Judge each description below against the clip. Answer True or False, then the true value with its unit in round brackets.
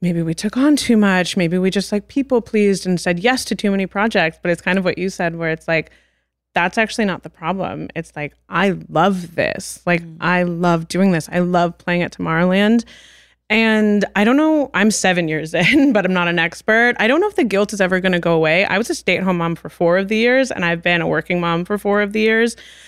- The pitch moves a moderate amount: True (3.7 semitones)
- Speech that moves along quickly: True (255 wpm)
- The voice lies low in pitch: False (185 Hz)